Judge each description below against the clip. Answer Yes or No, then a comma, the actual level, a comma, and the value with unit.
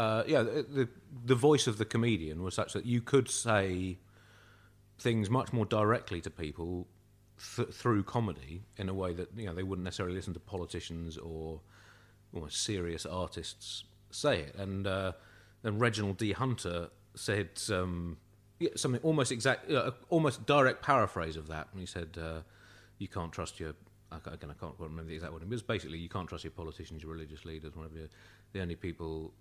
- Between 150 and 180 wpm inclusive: No, average, 195 wpm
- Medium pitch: No, low, 100 Hz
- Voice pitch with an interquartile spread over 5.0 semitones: No, average, 4.3 semitones